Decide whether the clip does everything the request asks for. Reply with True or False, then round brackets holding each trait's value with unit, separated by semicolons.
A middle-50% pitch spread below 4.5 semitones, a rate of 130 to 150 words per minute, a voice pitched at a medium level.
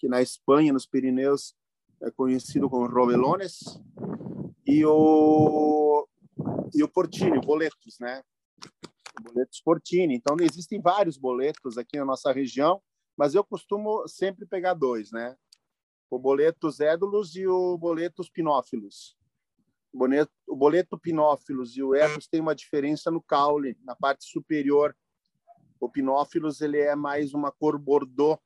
True (4.0 semitones; 140 wpm; 150 Hz)